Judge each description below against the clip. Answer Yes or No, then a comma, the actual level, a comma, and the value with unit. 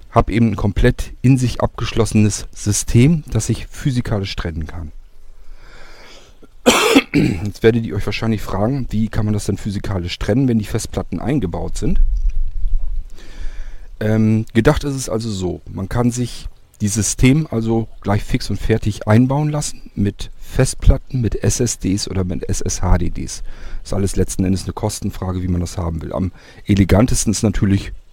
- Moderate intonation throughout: Yes, average, 3.9 semitones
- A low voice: Yes, low, 105 Hz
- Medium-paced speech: Yes, average, 155 wpm